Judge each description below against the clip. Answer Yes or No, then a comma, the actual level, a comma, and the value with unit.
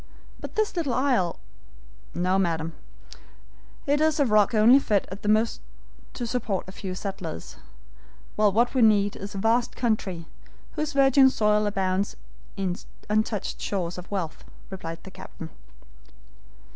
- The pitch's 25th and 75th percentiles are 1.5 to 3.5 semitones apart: No, average, 4.5 semitones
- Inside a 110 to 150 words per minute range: Yes, average, 145 wpm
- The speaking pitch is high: Yes, high, 205 Hz